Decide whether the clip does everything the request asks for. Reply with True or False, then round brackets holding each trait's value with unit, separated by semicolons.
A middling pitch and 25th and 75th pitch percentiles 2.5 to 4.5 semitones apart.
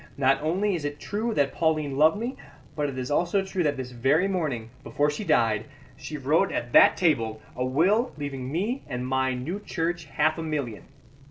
False (150 Hz; 5.1 semitones)